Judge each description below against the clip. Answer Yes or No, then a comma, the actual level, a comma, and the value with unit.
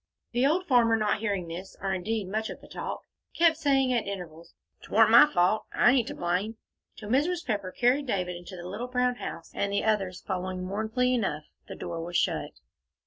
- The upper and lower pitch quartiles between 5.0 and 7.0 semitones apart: Yes, wide, 5.4 semitones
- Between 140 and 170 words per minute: No, average, 200 wpm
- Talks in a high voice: Yes, high, 215 Hz